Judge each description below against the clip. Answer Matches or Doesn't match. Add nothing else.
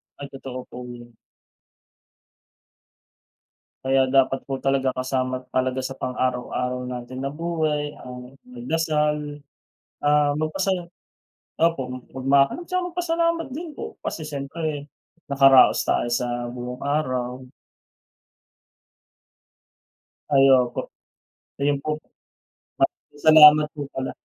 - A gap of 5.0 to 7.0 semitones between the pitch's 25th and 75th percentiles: Doesn't match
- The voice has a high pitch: Doesn't match